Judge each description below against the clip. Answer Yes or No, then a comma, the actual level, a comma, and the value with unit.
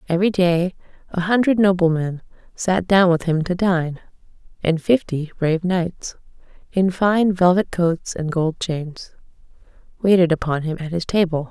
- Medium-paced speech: Yes, average, 150 wpm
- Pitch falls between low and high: Yes, medium, 175 Hz